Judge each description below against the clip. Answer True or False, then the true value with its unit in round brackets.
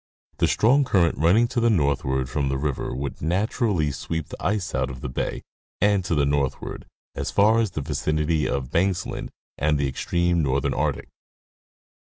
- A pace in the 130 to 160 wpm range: False (175 wpm)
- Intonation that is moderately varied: False (5.9 semitones)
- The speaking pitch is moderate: False (80 Hz)